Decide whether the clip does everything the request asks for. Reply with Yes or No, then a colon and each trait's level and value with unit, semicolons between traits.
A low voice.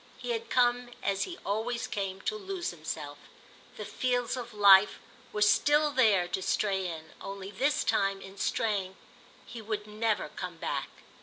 No: high, 210 Hz